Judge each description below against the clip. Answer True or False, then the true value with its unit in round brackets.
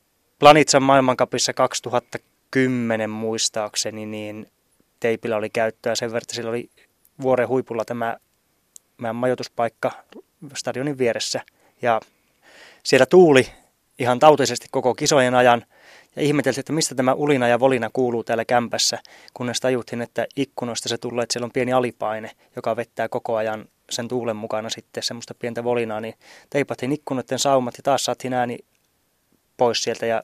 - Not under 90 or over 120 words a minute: False (145 wpm)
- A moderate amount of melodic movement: False (2.1 semitones)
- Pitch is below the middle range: True (120 Hz)